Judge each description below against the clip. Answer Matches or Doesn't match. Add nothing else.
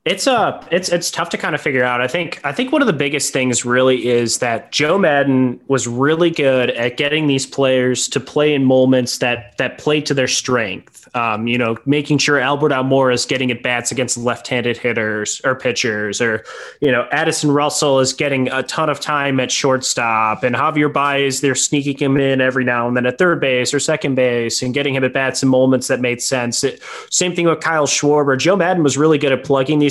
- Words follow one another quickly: Matches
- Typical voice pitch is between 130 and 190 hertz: Matches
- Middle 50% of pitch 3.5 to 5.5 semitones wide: Doesn't match